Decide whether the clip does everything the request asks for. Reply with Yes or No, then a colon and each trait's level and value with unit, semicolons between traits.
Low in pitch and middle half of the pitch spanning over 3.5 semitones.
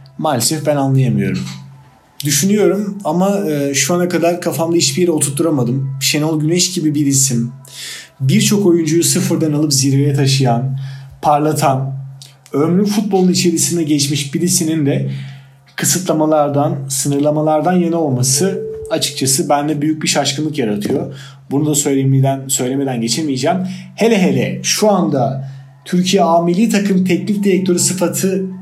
No: medium, 150 Hz; average, 4.2 semitones